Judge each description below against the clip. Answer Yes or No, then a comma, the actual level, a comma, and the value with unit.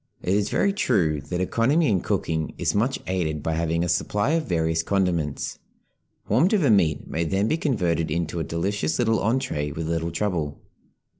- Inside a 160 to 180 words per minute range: Yes, average, 175 wpm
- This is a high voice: No, very low, 90 Hz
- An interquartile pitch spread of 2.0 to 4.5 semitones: No, average, 5.1 semitones